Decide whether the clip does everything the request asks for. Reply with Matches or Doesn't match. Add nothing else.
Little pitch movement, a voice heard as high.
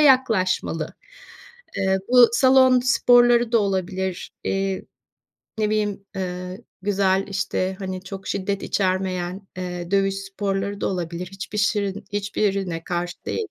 Matches